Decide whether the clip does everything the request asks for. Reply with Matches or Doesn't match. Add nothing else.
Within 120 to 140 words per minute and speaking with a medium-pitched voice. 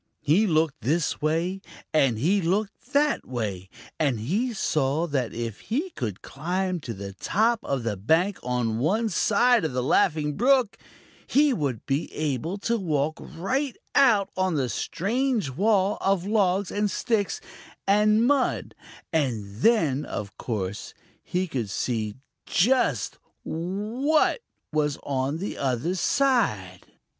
Matches